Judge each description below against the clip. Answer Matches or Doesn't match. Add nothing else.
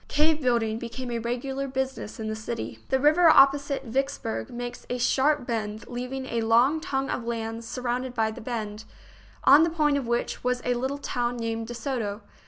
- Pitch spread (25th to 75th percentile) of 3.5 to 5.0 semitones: Doesn't match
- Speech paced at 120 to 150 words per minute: Doesn't match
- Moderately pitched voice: Doesn't match